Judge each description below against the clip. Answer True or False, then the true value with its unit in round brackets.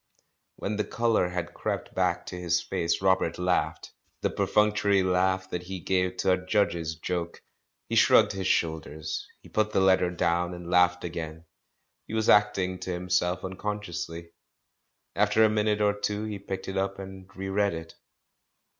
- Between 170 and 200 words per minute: True (175 wpm)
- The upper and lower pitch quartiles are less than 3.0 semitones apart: True (2.6 semitones)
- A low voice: True (95 Hz)